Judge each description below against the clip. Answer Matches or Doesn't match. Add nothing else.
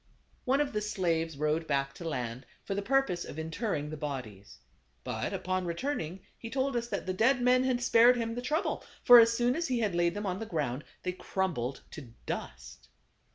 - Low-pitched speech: Doesn't match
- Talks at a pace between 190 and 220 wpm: Matches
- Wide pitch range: Matches